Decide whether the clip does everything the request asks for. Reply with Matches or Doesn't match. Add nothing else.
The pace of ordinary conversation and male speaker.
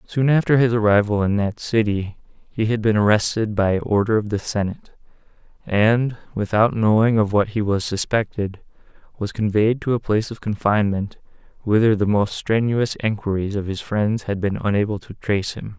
Matches